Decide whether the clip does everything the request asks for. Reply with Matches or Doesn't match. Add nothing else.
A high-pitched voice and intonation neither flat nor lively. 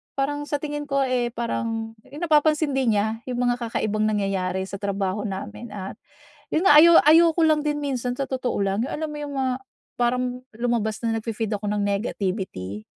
Doesn't match